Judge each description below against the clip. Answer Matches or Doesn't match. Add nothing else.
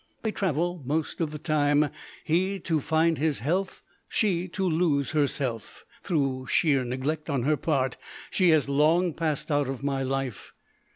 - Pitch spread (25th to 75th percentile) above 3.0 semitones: Matches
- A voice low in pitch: Doesn't match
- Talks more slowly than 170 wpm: Matches